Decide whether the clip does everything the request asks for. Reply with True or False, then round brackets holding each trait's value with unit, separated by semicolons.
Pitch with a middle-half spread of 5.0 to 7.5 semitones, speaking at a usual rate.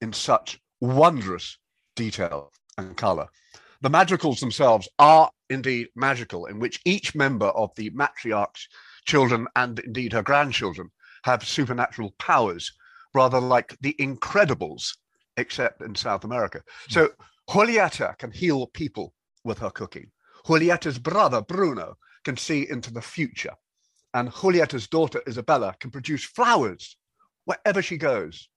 False (5.6 semitones; 130 wpm)